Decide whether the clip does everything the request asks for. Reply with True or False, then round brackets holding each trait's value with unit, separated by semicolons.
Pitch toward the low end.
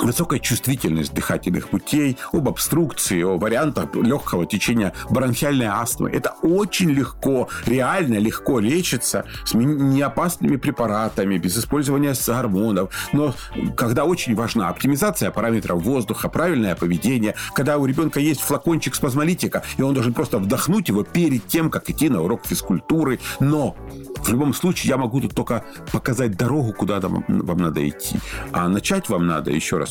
True (130 Hz)